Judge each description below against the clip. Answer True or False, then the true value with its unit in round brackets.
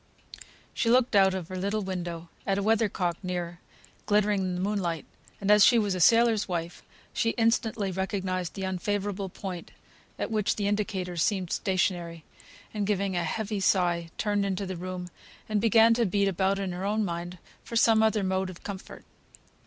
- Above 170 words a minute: True (180 wpm)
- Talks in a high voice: True (195 Hz)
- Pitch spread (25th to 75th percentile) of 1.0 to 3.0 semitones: True (2.6 semitones)